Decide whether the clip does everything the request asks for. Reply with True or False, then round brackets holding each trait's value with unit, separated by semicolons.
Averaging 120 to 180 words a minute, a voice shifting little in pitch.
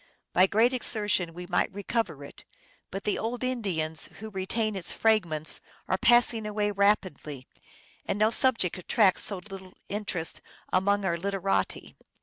False (150 wpm; 3.2 semitones)